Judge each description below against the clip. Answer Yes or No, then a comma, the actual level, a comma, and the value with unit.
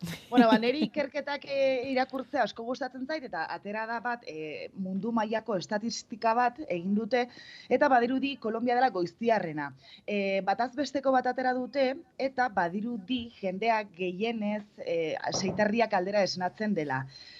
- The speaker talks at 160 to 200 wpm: No, average, 135 wpm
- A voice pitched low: No, high, 230 Hz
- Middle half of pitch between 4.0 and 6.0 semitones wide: Yes, average, 4.4 semitones